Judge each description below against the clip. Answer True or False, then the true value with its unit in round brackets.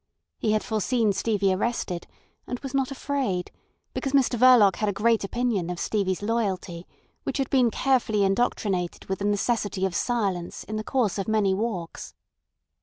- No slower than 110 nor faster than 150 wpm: False (165 wpm)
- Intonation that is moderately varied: True (4.0 semitones)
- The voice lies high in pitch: True (215 Hz)